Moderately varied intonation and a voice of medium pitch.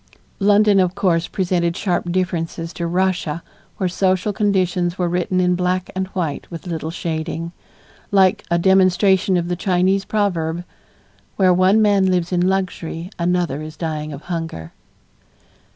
No: narrow, 2.0 semitones; medium, 180 Hz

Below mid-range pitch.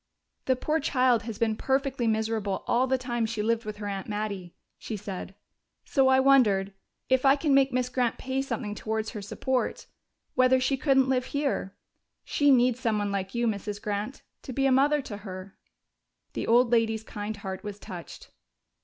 No: high, 230 Hz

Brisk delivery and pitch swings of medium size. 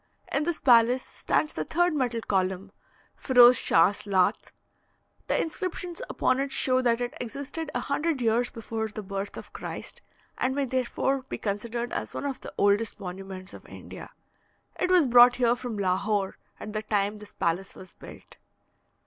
No: average, 165 wpm; average, 4.6 semitones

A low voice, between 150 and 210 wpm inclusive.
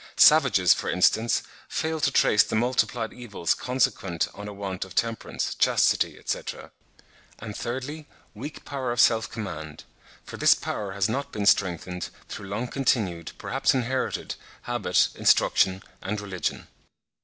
No: low, 110 Hz; average, 140 wpm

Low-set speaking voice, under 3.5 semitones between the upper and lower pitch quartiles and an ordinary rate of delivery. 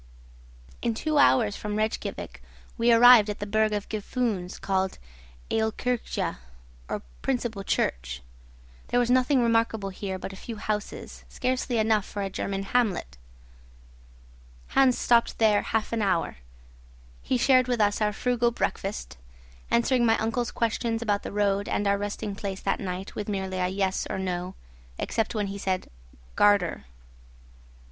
No: high, 210 Hz; average, 3.1 semitones; average, 145 wpm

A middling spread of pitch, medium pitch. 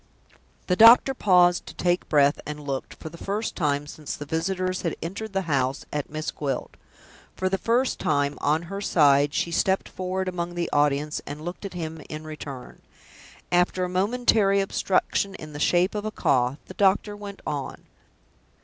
Yes: average, 4.6 semitones; medium, 175 Hz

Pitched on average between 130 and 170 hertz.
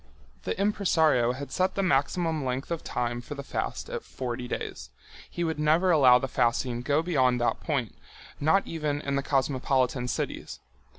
Yes: medium, 140 Hz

